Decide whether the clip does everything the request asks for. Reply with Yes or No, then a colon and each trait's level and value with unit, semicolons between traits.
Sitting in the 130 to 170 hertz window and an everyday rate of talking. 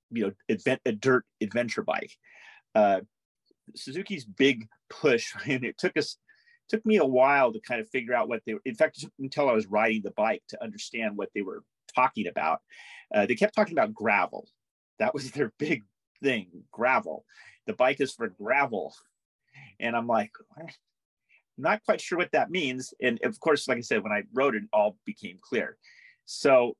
Yes: medium, 140 Hz; average, 185 wpm